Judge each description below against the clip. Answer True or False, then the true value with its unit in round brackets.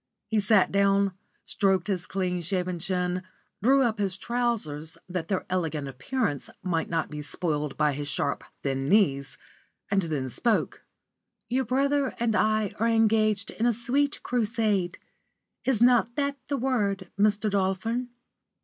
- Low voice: False (200 Hz)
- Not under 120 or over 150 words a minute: True (140 wpm)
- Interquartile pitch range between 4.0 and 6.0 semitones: True (4.8 semitones)